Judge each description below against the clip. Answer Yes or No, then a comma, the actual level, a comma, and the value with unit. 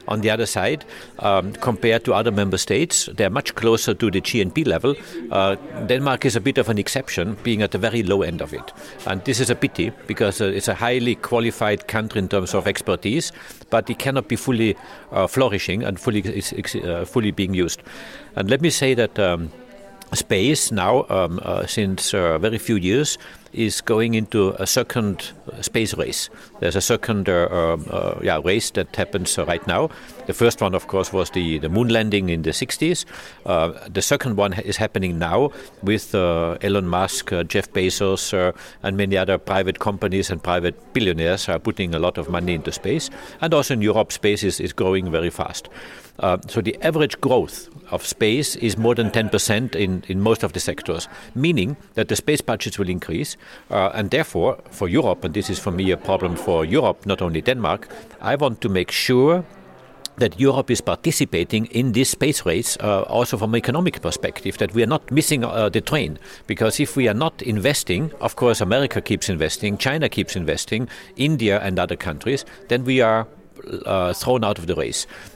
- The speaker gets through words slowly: No, average, 195 wpm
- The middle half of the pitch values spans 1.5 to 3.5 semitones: No, average, 3.9 semitones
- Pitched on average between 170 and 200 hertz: No, low, 105 Hz